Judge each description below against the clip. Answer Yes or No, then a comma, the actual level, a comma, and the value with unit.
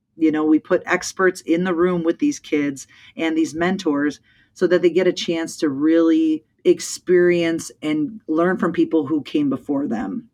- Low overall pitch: No, medium, 175 Hz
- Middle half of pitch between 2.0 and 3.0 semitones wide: Yes, average, 2.7 semitones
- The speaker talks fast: No, average, 180 wpm